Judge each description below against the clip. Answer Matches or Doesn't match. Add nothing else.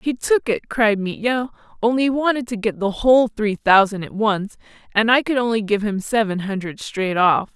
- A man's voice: Doesn't match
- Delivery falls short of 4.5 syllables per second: Doesn't match